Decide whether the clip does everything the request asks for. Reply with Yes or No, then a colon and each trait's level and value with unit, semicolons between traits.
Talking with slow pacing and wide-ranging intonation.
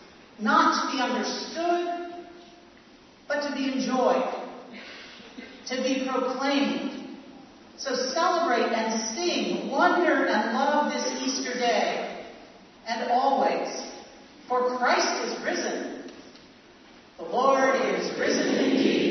No: slow, 100 wpm; narrow, 2.6 semitones